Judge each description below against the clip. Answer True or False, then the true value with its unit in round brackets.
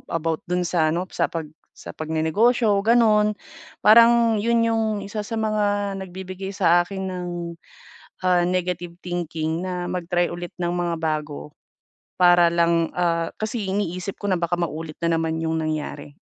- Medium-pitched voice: True (175 Hz)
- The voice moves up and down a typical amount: True (3.4 semitones)